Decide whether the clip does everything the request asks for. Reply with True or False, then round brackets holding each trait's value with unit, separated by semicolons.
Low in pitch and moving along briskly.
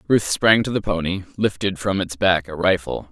True (95 Hz; 210 wpm)